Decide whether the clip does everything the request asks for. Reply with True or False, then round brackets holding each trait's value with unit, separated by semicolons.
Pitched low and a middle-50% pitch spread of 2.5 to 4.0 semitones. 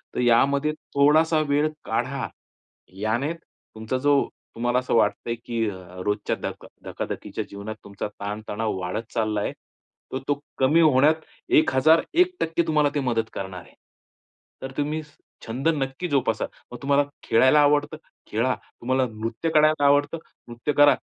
False (130 Hz; 4.7 semitones)